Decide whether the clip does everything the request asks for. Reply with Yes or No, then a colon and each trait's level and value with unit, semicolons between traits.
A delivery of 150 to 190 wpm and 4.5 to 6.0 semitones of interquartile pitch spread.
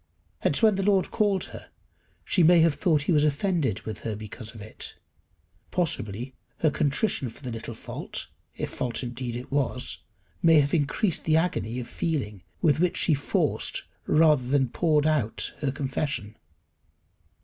Yes: average, 160 wpm; average, 5.2 semitones